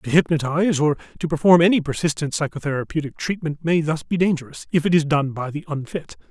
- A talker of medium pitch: Yes, medium, 155 Hz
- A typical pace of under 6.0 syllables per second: No, 6.2 syllables/s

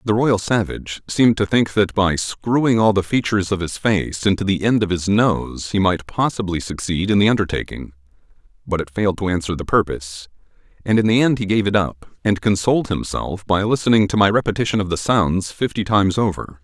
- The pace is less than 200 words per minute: No, fast, 205 wpm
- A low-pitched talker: Yes, low, 100 Hz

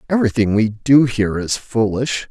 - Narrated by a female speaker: No, male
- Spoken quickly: No, average, 155 wpm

